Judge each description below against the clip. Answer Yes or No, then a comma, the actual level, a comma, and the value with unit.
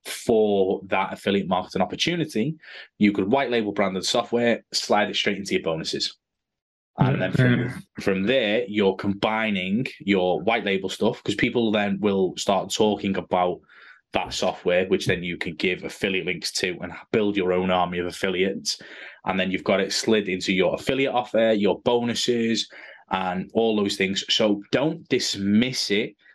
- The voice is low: Yes, low, 105 Hz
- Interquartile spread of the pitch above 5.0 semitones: No, average, 3.6 semitones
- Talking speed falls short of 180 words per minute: Yes, average, 165 wpm